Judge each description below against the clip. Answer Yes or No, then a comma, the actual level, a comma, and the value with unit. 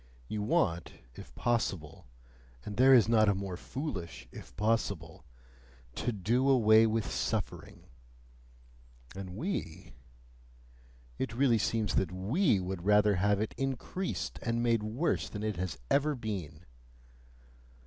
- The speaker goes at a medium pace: No, slow, 130 wpm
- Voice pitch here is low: Yes, low, 110 Hz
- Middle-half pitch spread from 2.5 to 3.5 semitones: No, average, 4.1 semitones